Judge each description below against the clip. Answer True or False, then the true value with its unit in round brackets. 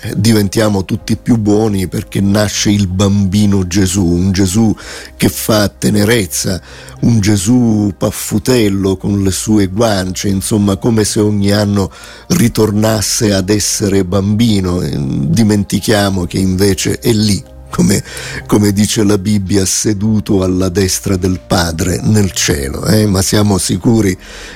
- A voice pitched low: True (100 Hz)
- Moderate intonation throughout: False (1.8 semitones)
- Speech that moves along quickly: False (125 wpm)